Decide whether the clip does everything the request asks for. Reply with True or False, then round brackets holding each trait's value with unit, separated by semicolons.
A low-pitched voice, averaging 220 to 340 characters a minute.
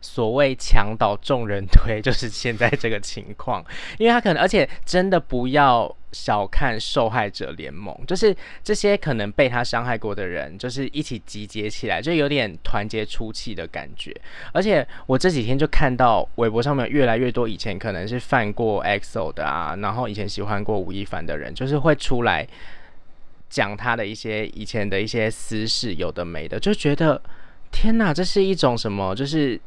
True (120 Hz; 280 characters per minute)